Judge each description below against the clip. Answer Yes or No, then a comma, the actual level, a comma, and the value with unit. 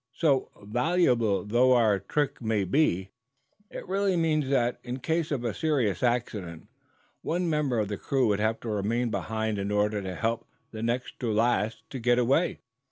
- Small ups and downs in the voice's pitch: No, average, 4.5 semitones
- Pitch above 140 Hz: No, low, 120 Hz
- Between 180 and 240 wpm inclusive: No, average, 170 wpm